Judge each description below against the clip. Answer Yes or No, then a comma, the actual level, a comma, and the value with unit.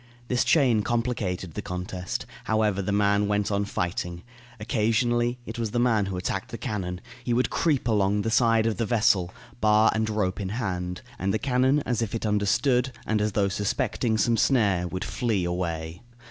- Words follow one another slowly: No, average, 185 wpm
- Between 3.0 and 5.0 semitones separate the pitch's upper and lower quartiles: Yes, average, 3.6 semitones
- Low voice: Yes, low, 105 Hz